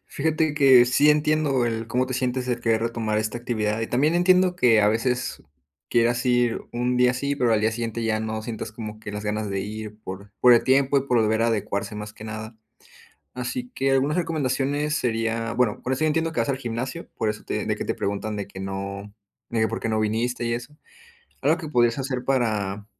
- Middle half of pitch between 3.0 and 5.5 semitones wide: Yes, average, 3.4 semitones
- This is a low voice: Yes, low, 120 Hz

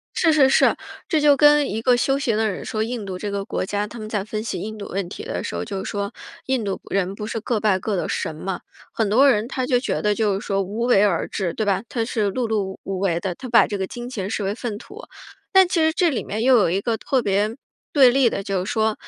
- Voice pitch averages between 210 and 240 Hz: Yes, high, 215 Hz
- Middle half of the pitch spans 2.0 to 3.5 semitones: No, average, 4.0 semitones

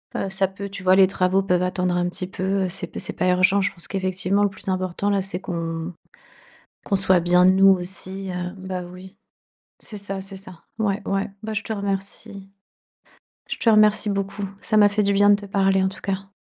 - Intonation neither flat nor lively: No, narrow, 1.5 semitones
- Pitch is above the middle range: Yes, high, 195 Hz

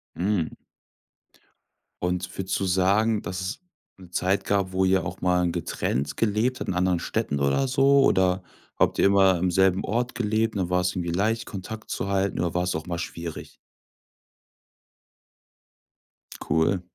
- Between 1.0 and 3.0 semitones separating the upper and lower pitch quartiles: Yes, narrow, 2.6 semitones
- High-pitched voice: No, very low, 95 Hz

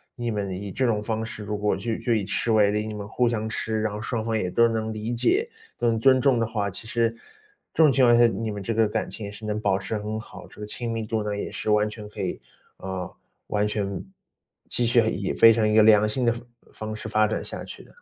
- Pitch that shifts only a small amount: Yes, narrow, 1.8 semitones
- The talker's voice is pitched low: Yes, low, 110 Hz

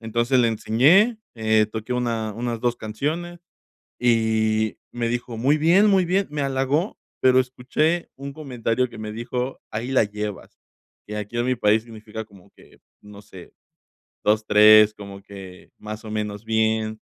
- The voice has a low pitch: Yes, low, 115 Hz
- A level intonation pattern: No, average, 3.2 semitones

